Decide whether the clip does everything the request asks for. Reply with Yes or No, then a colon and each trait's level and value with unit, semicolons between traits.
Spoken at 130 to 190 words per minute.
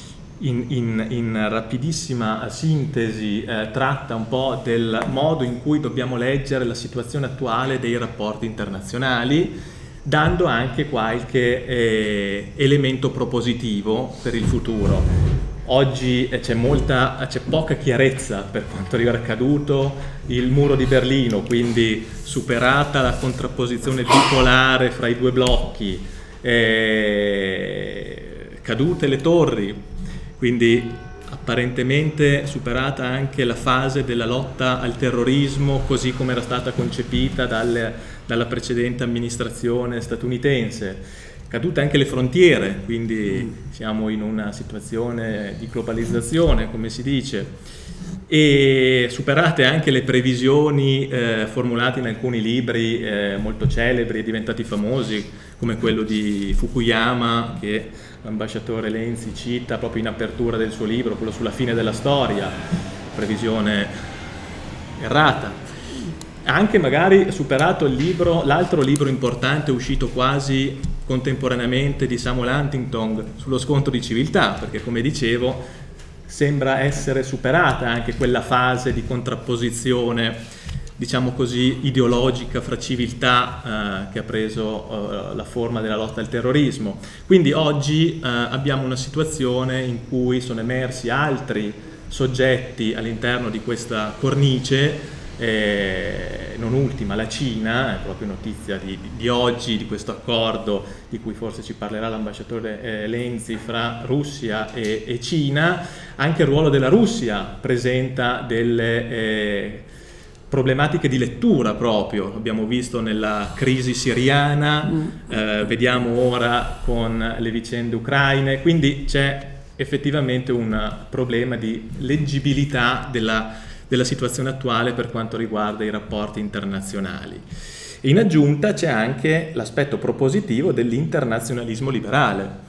No: average, 120 wpm